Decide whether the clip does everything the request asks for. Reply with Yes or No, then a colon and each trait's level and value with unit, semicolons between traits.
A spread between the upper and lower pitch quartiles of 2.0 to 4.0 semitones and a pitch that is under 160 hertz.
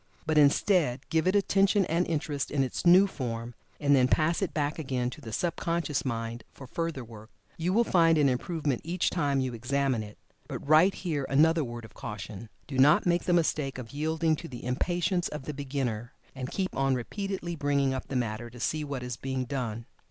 No: average, 4.9 semitones; medium, 140 Hz